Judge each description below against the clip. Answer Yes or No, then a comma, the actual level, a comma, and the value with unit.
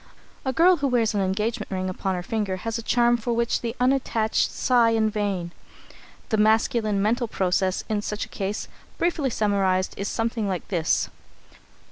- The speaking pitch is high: Yes, high, 215 Hz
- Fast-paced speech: No, average, 170 wpm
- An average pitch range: Yes, average, 3.3 semitones